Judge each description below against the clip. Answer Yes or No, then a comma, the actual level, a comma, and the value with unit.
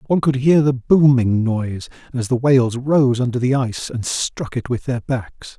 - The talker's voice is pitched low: Yes, low, 125 Hz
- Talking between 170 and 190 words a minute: No, fast, 205 wpm